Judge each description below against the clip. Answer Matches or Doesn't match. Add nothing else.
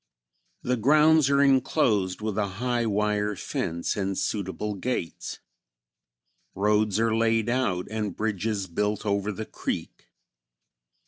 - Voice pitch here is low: Matches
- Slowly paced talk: Matches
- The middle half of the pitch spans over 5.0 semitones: Doesn't match